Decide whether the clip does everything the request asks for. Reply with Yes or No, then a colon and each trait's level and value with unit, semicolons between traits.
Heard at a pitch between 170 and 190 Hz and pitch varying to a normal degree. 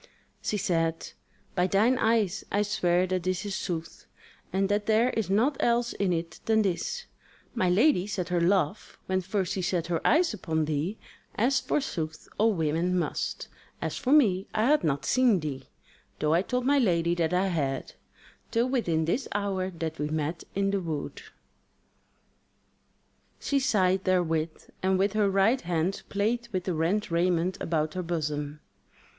Yes: medium, 185 Hz; average, 4.3 semitones